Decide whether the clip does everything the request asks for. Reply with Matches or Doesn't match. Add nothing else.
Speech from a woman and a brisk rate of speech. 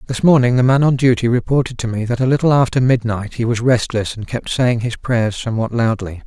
Doesn't match